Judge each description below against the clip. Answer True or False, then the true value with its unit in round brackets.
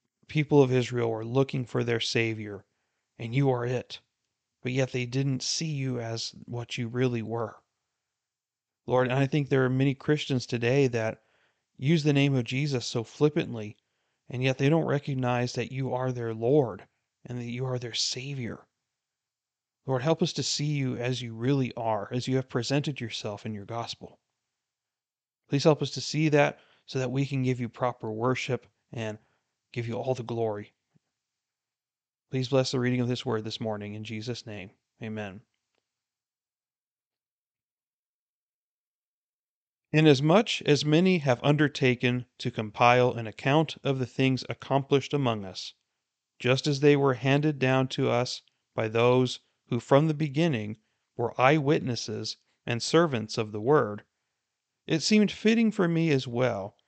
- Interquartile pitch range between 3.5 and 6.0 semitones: False (3.0 semitones)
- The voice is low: True (125 Hz)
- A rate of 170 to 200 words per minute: False (160 wpm)